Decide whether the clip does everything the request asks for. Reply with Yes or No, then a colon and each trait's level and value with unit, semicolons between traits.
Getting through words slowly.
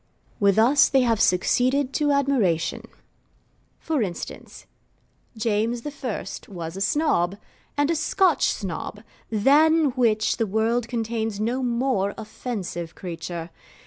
Yes: slow, 115 wpm